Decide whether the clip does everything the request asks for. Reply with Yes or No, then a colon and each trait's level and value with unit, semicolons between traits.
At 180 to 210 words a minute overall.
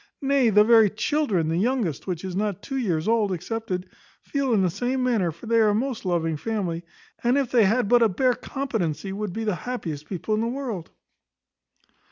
Yes: fast, 205 wpm